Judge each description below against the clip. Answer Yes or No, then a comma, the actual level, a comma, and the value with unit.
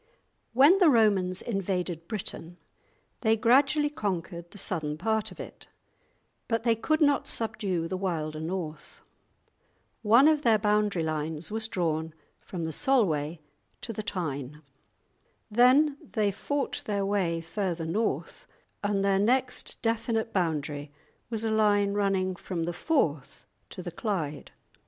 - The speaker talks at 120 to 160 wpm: Yes, slow, 135 wpm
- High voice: Yes, high, 200 Hz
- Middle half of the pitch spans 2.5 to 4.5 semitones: No, average, 5.3 semitones